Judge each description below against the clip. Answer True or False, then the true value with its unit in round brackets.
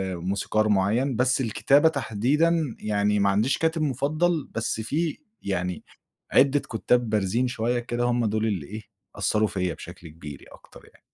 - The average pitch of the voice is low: True (115 Hz)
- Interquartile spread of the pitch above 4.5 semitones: True (5.1 semitones)